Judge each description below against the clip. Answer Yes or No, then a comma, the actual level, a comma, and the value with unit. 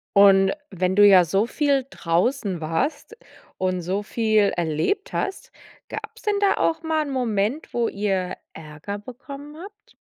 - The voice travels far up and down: Yes, wide, 7.2 semitones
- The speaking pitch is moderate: No, high, 205 Hz